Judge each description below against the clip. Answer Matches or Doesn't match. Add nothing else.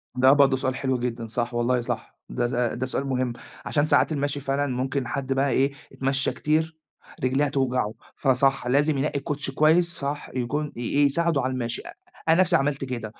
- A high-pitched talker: Doesn't match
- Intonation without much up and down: Matches